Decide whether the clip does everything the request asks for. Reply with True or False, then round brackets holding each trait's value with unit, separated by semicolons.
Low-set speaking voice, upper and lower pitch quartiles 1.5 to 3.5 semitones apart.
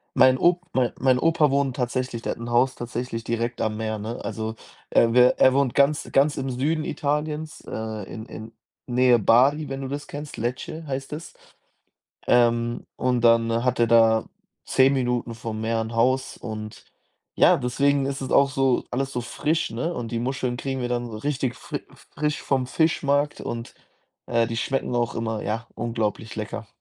True (125 Hz; 2.9 semitones)